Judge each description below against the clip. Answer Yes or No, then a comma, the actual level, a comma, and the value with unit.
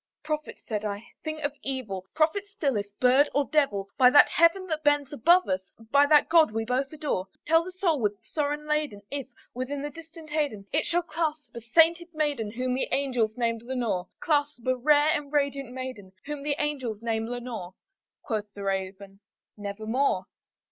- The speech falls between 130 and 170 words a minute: No, average, 180 wpm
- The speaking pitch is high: Yes, very high, 275 Hz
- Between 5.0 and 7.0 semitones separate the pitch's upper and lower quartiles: Yes, average, 5.3 semitones